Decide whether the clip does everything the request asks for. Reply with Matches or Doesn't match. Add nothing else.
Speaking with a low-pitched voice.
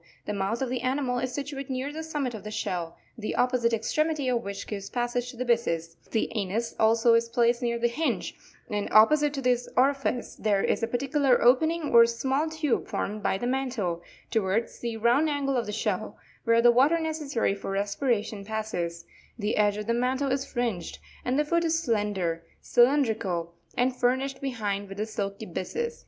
Doesn't match